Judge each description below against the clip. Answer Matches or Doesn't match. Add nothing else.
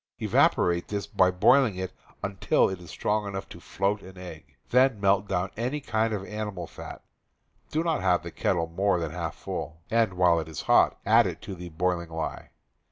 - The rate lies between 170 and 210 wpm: Matches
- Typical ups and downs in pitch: Matches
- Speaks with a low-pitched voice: Matches